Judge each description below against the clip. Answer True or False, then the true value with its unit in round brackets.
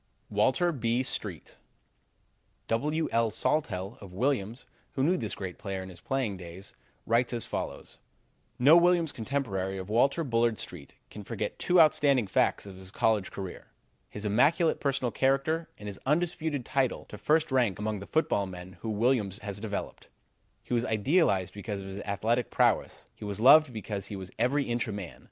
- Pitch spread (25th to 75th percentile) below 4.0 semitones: False (5.5 semitones)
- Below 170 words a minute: False (175 wpm)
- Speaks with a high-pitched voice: False (115 Hz)